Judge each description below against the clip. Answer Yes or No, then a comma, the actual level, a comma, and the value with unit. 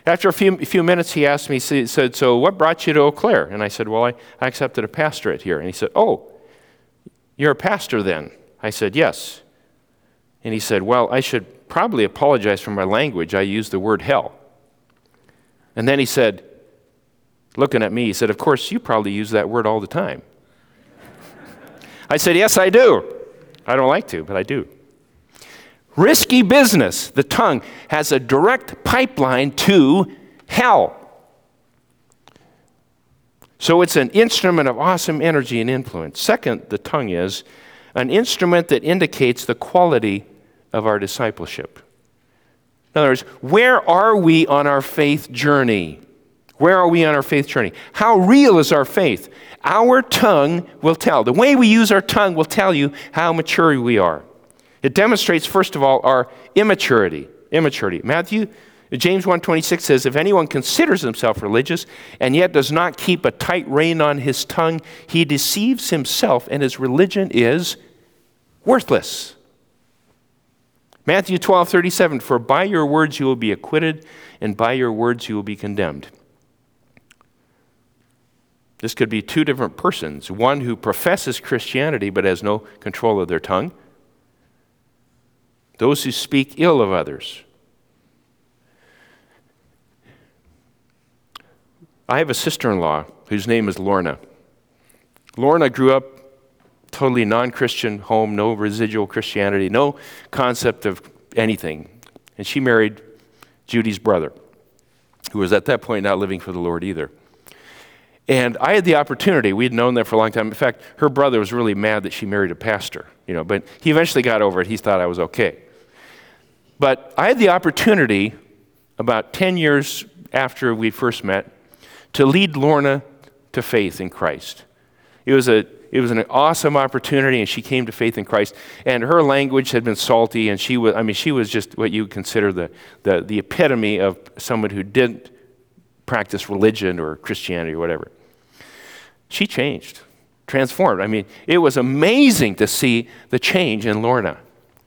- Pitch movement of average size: No, wide, 6.6 semitones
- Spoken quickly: No, average, 160 wpm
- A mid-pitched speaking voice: No, low, 130 Hz